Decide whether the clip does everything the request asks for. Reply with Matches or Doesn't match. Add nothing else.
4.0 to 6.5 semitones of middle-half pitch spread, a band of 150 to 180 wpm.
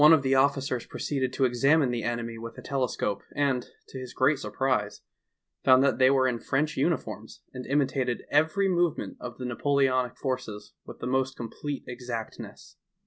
Doesn't match